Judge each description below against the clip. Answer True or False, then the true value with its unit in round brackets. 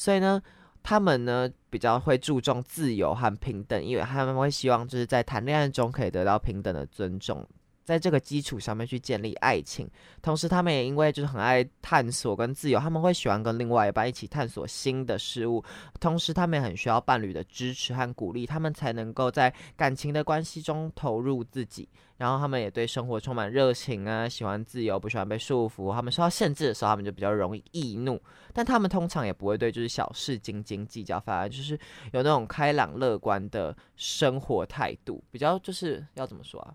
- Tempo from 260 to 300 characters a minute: False (325 characters per minute)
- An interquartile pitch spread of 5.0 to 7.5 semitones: False (4.5 semitones)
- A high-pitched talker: False (125 Hz)